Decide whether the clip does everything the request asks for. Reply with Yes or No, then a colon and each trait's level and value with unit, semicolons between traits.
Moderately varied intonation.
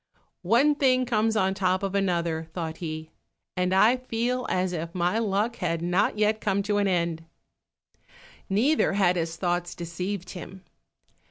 Yes: average, 3.6 semitones